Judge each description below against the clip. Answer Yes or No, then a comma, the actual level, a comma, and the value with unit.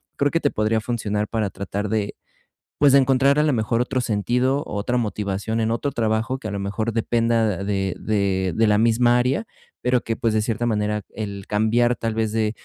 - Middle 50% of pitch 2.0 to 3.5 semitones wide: Yes, narrow, 2.6 semitones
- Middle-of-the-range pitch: No, low, 110 Hz